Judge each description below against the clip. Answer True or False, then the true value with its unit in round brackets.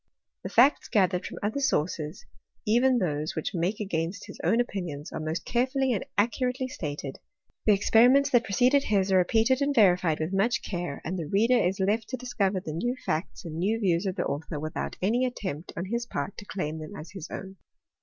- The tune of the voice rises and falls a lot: True (5.9 semitones)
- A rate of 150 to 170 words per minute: False (200 wpm)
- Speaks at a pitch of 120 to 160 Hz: False (195 Hz)